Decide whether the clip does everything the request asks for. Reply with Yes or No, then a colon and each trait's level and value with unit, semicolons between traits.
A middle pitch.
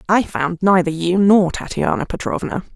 Yes: medium, 180 Hz